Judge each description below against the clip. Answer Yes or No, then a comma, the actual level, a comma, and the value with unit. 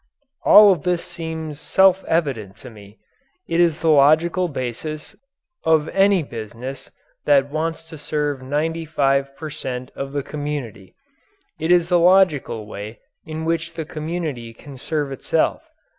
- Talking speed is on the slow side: No, average, 145 wpm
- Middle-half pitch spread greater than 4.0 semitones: No, average, 3.3 semitones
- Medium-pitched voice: Yes, medium, 150 Hz